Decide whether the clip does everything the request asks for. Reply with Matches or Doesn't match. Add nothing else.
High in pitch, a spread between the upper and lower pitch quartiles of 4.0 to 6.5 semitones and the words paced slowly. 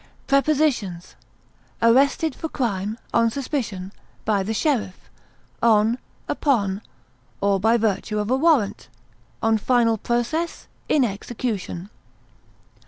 Matches